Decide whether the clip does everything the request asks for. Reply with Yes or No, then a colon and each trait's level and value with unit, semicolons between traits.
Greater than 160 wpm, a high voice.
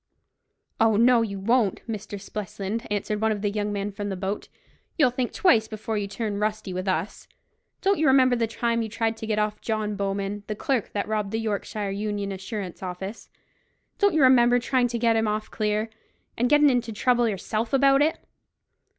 Yes: average, 190 wpm; high, 215 Hz